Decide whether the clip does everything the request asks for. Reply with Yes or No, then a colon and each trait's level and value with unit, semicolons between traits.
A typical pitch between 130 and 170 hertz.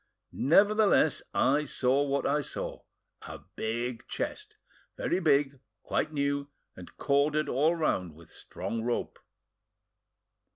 Yes: medium, 140 Hz